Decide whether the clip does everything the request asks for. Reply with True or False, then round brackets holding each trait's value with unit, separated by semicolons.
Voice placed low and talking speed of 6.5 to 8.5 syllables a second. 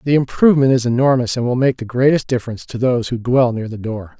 True (125 Hz; 6.6 syllables/s)